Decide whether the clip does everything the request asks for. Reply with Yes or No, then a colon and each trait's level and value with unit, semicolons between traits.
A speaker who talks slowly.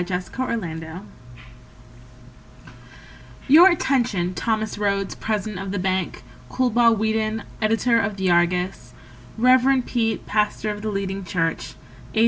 Yes: slow, 115 wpm